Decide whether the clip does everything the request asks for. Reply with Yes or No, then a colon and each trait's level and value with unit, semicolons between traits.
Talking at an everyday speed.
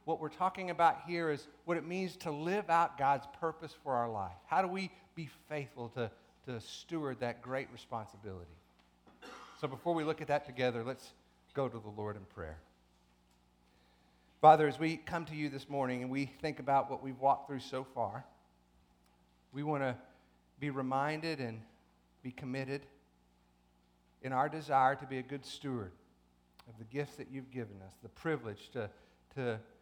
Yes: average, 175 wpm